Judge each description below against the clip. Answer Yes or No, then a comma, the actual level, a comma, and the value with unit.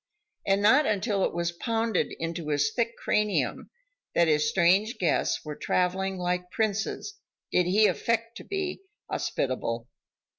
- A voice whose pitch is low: No, high, 190 Hz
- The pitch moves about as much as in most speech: Yes, average, 4.6 semitones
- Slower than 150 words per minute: Yes, average, 140 wpm